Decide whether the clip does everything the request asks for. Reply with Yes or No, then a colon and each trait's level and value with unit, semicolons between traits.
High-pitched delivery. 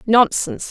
Yes: high, 235 Hz